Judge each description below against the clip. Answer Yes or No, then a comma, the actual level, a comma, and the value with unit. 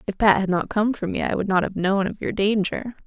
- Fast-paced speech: Yes, fast, 295 wpm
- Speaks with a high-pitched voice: Yes, high, 200 Hz